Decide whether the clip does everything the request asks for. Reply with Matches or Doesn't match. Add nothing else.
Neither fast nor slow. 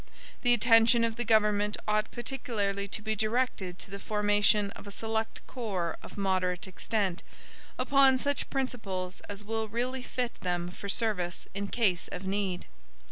Matches